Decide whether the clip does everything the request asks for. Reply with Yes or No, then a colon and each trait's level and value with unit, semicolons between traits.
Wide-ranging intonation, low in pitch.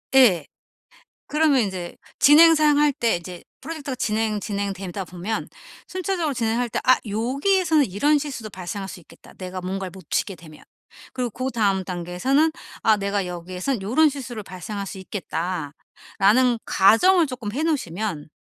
No: wide, 6.8 semitones; high, 215 Hz